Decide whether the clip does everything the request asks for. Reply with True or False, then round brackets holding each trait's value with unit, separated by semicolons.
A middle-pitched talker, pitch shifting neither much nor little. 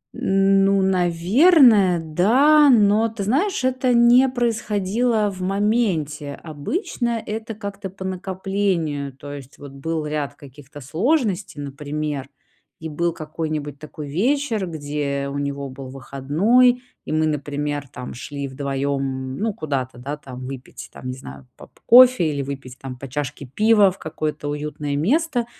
False (160 Hz; 7.0 semitones)